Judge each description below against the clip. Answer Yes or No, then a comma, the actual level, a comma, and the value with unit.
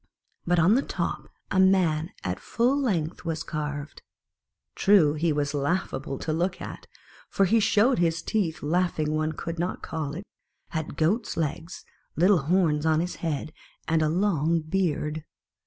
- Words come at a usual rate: Yes, average, 155 wpm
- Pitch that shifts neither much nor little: Yes, average, 3.4 semitones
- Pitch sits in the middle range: Yes, medium, 165 Hz